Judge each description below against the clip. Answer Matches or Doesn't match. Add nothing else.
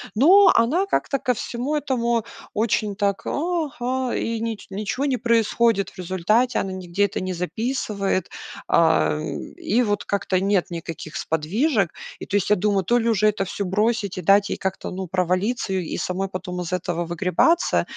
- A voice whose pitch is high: Matches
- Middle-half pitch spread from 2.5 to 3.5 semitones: Doesn't match